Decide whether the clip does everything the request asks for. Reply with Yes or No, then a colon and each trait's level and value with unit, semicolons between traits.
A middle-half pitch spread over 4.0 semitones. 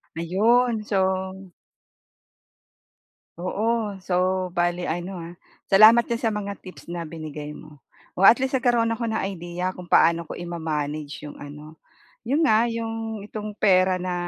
Yes: average, 4.5 semitones